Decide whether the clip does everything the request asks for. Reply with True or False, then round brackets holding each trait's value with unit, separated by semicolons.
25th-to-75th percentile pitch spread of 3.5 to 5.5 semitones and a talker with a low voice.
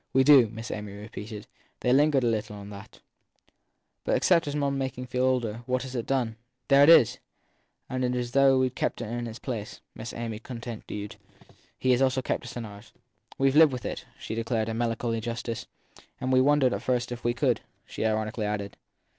False (2.7 semitones; 120 Hz)